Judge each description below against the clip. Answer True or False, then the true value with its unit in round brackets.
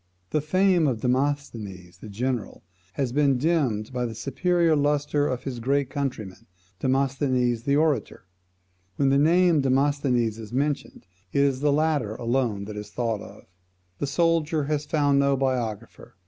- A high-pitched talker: False (135 Hz)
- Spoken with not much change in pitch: False (3.6 semitones)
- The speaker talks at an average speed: True (155 wpm)